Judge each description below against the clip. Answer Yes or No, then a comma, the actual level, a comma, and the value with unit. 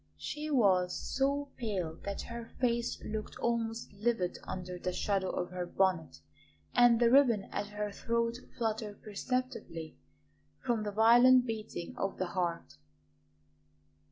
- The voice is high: Yes, high, 215 Hz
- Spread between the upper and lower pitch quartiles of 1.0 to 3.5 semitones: No, average, 4.2 semitones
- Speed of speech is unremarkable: No, slow, 130 wpm